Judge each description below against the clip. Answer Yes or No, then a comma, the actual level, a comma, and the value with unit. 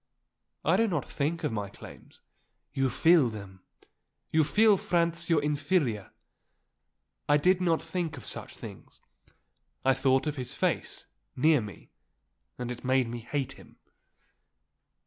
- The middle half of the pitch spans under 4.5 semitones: No, average, 5.1 semitones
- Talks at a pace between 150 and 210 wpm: No, average, 140 wpm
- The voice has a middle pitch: Yes, medium, 145 Hz